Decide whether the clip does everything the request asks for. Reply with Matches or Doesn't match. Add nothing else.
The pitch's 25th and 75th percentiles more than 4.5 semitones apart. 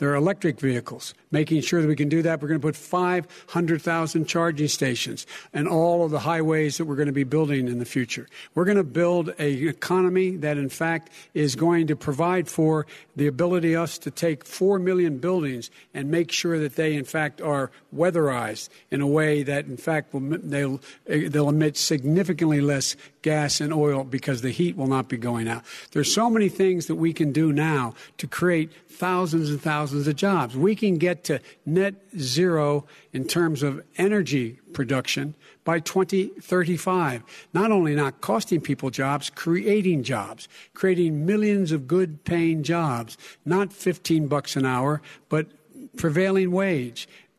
Doesn't match